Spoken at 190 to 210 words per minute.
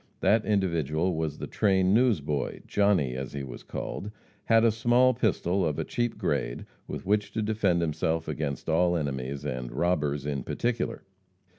No: average, 160 wpm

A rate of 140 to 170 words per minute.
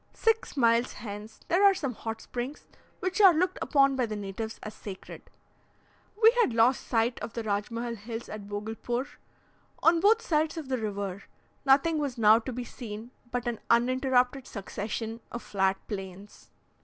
Yes: average, 165 wpm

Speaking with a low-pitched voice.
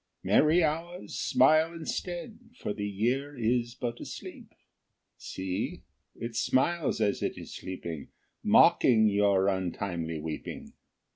Yes: low, 115 Hz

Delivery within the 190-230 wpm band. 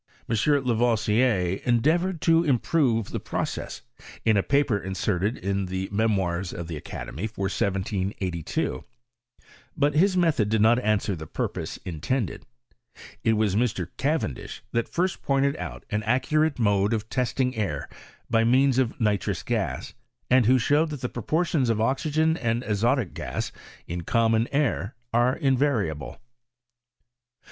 No: average, 140 wpm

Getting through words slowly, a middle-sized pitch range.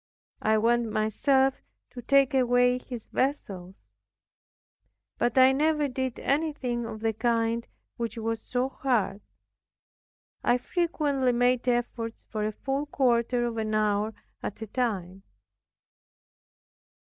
Yes: slow, 120 wpm; average, 3.0 semitones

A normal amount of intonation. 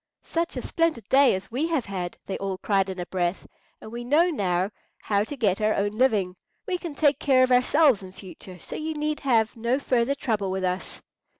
No: wide, 6.7 semitones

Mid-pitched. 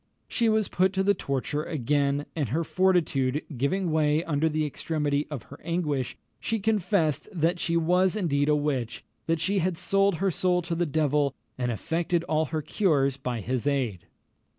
Yes: medium, 155 Hz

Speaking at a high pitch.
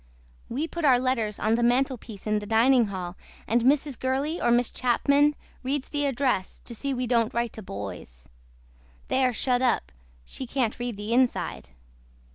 Yes: high, 245 Hz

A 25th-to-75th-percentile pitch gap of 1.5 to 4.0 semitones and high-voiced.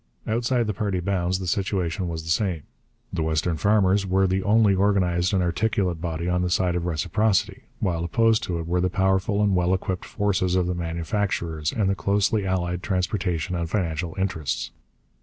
No: narrow, 2.4 semitones; very low, 90 Hz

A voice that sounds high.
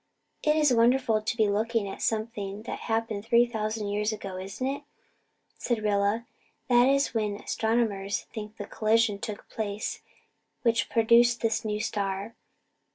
Yes: high, 220 Hz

